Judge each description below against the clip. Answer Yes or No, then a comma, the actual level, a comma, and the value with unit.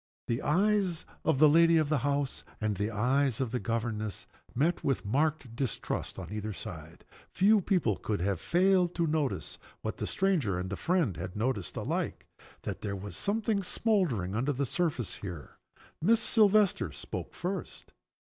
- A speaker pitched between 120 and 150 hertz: Yes, medium, 140 Hz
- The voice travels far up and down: Yes, wide, 8.8 semitones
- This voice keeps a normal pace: Yes, average, 165 wpm